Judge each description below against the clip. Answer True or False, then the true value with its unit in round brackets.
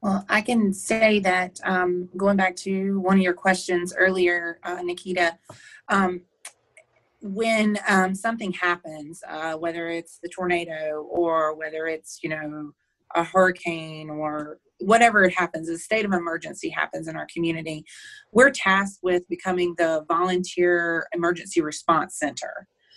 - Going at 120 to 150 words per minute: True (140 wpm)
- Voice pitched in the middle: True (180 Hz)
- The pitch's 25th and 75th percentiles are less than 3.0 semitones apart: True (2.5 semitones)